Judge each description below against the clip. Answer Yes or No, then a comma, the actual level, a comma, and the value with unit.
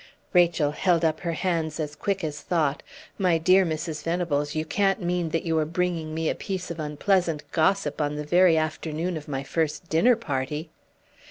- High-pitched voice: No, medium, 160 Hz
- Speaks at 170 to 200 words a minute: Yes, average, 185 wpm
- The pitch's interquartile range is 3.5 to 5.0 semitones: No, narrow, 2.6 semitones